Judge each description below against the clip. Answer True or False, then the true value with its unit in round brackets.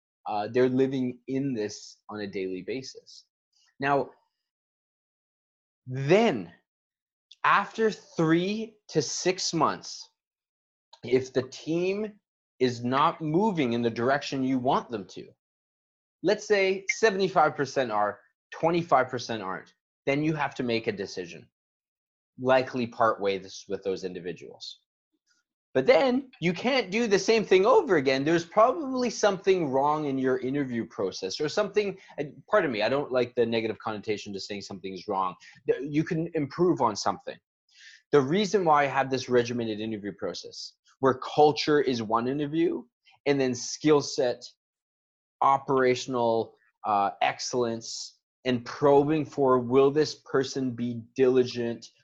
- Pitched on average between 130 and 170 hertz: True (135 Hz)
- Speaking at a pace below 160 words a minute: True (135 wpm)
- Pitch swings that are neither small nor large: False (7.8 semitones)